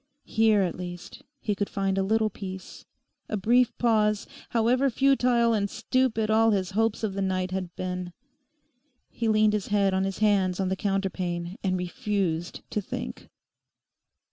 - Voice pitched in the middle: No, high, 200 Hz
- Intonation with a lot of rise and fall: No, average, 2.9 semitones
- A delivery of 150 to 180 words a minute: Yes, average, 160 wpm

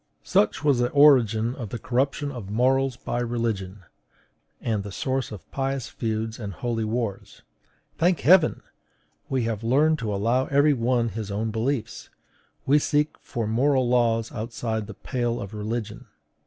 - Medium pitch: No, low, 120 Hz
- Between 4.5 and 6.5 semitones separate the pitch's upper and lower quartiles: No, average, 3.3 semitones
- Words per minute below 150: No, average, 155 wpm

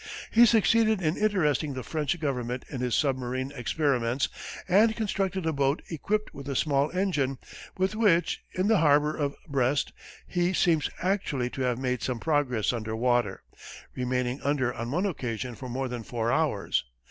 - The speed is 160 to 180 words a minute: Yes, average, 165 wpm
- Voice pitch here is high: No, medium, 140 Hz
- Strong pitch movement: Yes, wide, 5.8 semitones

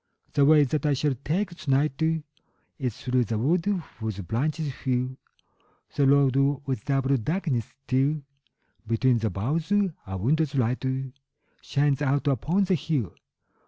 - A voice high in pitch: No, low, 135 Hz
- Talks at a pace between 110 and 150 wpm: Yes, average, 140 wpm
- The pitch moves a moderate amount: Yes, average, 3.4 semitones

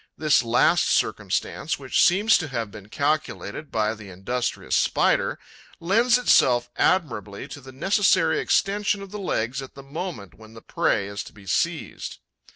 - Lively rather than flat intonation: Yes, wide, 8.7 semitones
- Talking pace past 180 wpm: No, average, 160 wpm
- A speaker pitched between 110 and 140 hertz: Yes, low, 135 Hz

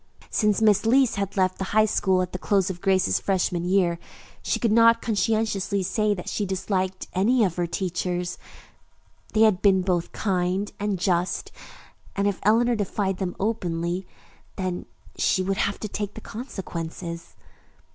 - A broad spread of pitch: No, narrow, 2.6 semitones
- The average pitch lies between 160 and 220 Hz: Yes, high, 190 Hz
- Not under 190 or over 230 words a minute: No, average, 160 wpm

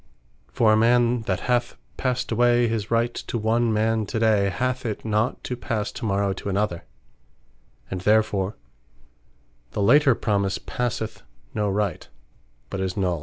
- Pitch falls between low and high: No, low, 110 Hz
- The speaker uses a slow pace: No, average, 155 wpm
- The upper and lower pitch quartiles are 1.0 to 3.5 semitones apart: Yes, average, 3.0 semitones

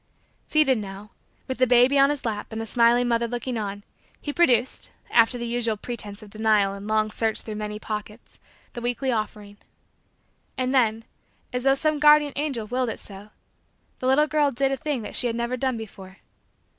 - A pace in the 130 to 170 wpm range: No, average, 190 wpm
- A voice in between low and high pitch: No, high, 235 Hz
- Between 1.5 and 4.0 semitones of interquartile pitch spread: Yes, average, 3.5 semitones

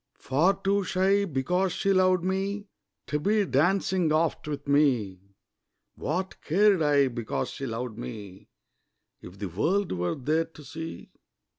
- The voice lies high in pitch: No, medium, 160 Hz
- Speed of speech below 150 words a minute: Yes, average, 140 wpm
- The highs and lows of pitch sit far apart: Yes, wide, 6.4 semitones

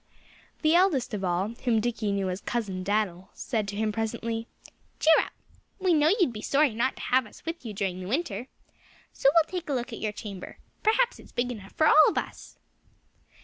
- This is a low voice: No, high, 230 Hz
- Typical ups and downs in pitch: No, wide, 6.5 semitones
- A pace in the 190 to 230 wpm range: Yes, fast, 205 wpm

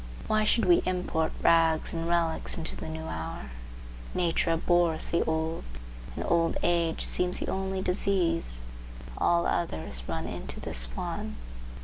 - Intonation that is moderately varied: No, narrow, 1.9 semitones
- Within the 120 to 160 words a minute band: Yes, average, 140 wpm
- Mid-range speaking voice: Yes, medium, 165 Hz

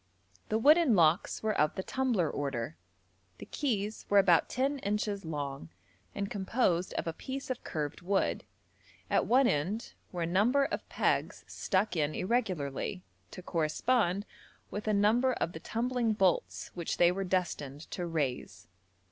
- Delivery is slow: No, average, 155 wpm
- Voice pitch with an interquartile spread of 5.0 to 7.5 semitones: Yes, wide, 5.5 semitones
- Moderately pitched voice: No, high, 195 Hz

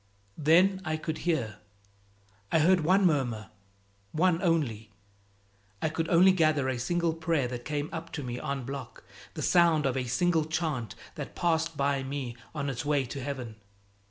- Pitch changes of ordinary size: Yes, average, 4.0 semitones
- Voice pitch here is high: No, medium, 150 Hz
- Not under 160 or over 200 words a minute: Yes, average, 165 wpm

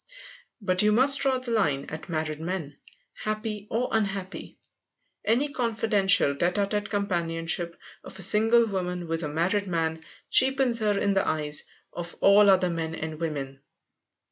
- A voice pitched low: No, high, 190 Hz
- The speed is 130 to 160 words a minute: Yes, average, 155 wpm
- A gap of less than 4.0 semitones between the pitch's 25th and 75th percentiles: No, average, 4.6 semitones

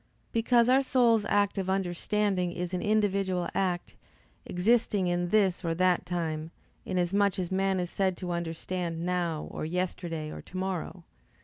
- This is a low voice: No, medium, 185 Hz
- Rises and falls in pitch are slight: Yes, narrow, 2.3 semitones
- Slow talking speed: No, average, 150 wpm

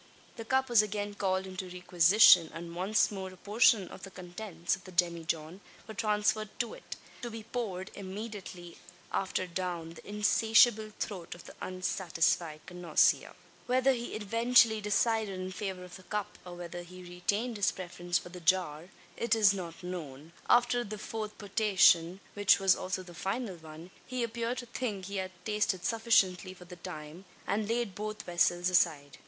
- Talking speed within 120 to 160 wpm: No, average, 170 wpm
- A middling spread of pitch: Yes, average, 3.4 semitones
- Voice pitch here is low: No, high, 190 Hz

